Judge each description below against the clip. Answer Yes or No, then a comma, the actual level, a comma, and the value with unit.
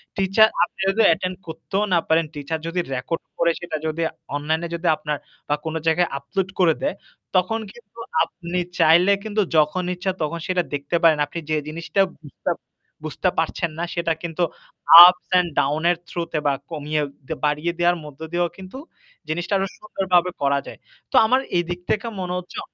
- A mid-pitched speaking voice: Yes, medium, 170 Hz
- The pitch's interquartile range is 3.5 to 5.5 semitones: No, narrow, 2.6 semitones